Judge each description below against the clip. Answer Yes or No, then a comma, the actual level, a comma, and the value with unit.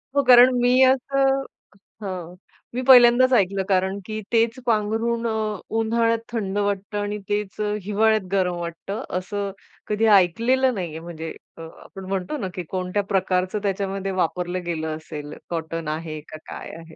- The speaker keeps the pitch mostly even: No, average, 4.1 semitones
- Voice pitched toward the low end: No, high, 200 Hz